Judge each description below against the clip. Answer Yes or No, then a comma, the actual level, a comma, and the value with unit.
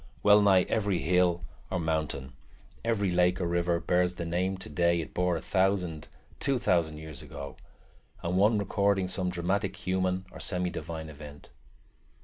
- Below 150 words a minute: No, average, 155 wpm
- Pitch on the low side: Yes, very low, 90 Hz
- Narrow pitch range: Yes, narrow, 2.2 semitones